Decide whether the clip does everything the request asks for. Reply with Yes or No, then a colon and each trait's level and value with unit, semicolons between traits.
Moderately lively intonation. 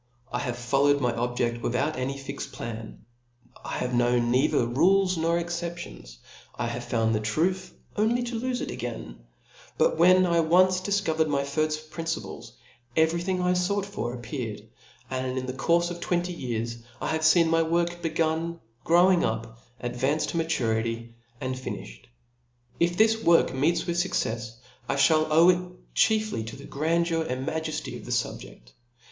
No: wide, 6.1 semitones